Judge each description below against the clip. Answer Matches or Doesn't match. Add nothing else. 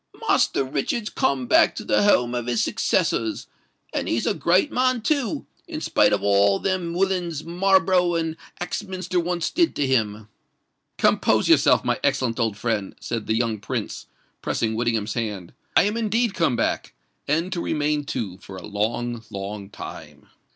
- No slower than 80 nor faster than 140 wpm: Doesn't match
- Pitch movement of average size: Doesn't match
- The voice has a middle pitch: Matches